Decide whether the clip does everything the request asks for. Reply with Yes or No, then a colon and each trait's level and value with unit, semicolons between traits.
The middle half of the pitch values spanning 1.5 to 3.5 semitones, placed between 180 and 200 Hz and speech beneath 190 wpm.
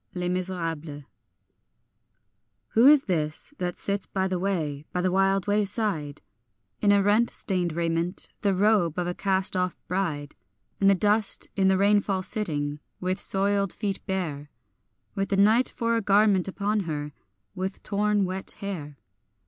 Yes: average, 2.8 semitones; high, 190 Hz; average, 150 wpm